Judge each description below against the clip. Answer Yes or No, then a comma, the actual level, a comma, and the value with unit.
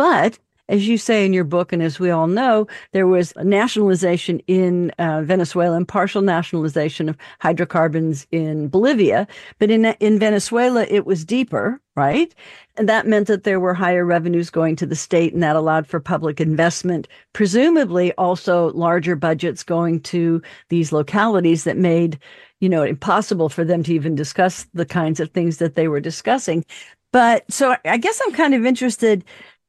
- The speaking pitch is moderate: Yes, medium, 175 Hz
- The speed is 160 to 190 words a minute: Yes, average, 175 wpm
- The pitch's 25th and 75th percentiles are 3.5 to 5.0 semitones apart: Yes, average, 4.0 semitones